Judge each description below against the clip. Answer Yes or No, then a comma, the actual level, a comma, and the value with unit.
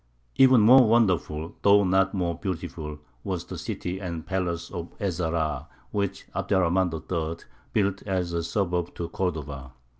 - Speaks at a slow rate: No, average, 155 wpm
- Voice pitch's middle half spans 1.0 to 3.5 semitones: Yes, average, 2.7 semitones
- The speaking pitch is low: Yes, very low, 90 Hz